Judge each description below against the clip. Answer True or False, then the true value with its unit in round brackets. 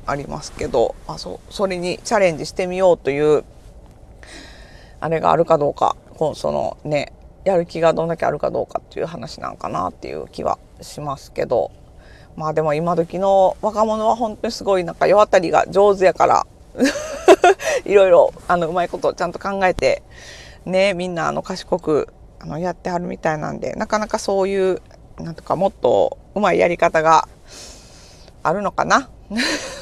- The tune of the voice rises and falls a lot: False (4.0 semitones)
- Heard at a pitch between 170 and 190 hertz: True (185 Hz)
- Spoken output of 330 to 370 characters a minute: True (335 characters per minute)